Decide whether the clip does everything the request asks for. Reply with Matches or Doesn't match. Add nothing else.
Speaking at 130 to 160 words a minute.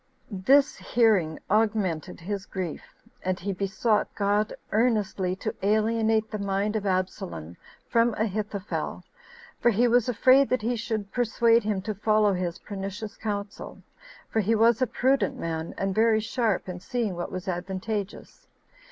Matches